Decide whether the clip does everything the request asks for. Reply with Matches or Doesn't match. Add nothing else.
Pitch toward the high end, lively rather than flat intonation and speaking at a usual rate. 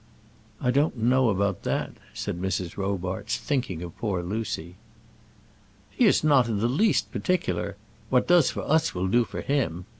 Doesn't match